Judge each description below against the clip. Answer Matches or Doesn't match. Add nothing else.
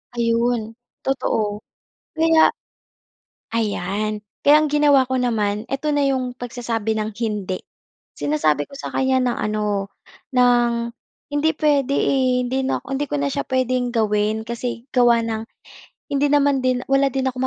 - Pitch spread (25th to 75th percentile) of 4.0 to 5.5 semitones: Doesn't match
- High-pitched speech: Matches